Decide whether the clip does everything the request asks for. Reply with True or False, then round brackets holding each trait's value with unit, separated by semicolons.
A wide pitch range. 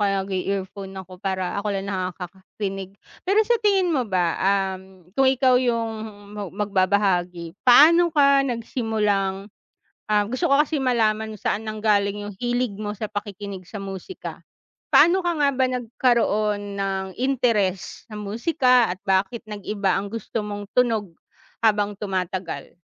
False (3.9 semitones)